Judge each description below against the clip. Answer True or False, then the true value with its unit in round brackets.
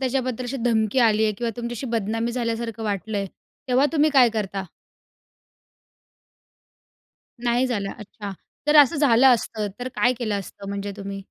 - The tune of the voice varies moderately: True (3.3 semitones)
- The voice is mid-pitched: False (230 Hz)